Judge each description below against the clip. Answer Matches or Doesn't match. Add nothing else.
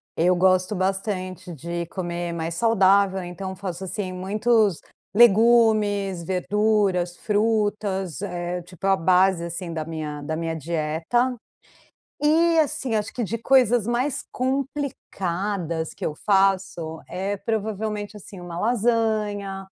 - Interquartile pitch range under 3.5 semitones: Doesn't match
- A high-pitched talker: Matches